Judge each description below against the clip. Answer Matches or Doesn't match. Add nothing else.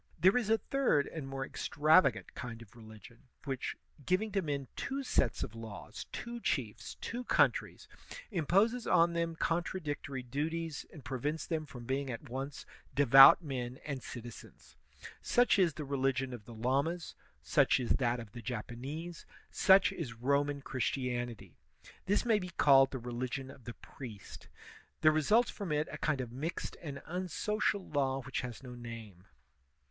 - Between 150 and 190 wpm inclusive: Matches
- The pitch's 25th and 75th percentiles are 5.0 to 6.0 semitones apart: Matches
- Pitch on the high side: Doesn't match